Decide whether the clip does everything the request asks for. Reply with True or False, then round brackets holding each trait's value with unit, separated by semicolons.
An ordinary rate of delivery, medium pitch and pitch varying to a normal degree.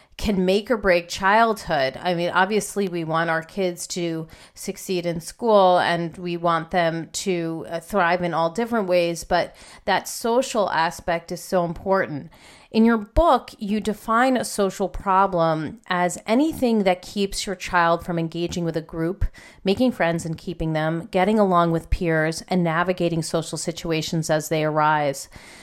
True (160 wpm; 175 Hz; 3.2 semitones)